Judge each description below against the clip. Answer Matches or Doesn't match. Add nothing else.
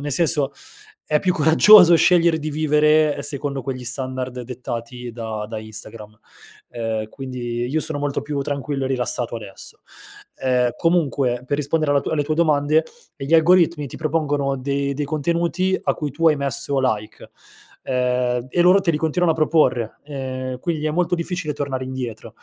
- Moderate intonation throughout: Matches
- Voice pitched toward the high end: Doesn't match